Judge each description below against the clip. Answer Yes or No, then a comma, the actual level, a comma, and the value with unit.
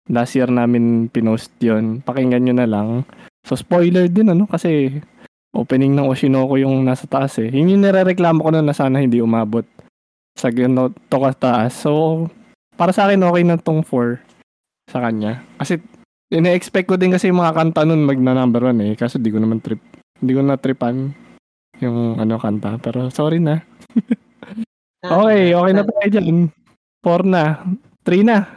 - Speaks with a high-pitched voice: No, low, 135 Hz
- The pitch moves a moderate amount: No, wide, 6.4 semitones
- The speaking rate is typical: No, fast, 175 wpm